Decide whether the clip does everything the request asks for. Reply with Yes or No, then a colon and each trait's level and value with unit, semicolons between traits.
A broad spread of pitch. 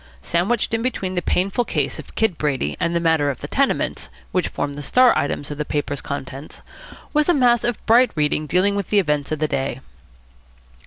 Yes: wide, 7.6 semitones